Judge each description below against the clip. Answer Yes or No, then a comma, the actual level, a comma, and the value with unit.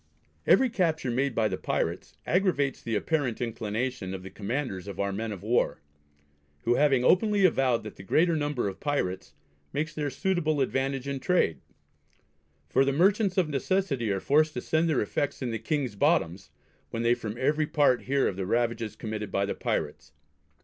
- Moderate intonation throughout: No, wide, 5.9 semitones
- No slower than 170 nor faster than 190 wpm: Yes, average, 180 wpm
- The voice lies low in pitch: Yes, low, 130 Hz